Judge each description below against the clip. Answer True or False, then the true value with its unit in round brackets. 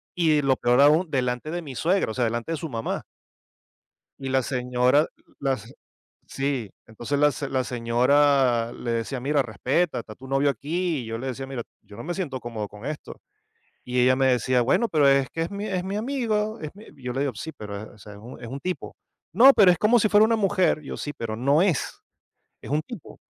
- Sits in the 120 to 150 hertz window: True (135 Hz)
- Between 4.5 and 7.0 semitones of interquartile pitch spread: True (5.1 semitones)